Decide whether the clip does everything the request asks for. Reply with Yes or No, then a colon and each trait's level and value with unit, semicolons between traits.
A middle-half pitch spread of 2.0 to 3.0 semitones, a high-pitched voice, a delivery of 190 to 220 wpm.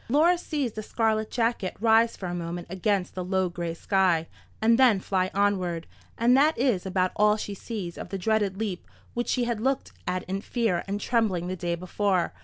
No: average, 3.9 semitones; high, 200 Hz; average, 200 wpm